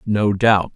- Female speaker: No, male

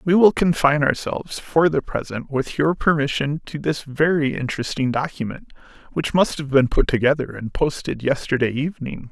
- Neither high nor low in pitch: Yes, medium, 145 Hz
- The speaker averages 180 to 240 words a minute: No, average, 165 wpm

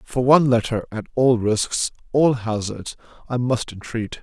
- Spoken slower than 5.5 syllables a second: Yes, 4.3 syllables/s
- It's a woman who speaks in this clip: No, male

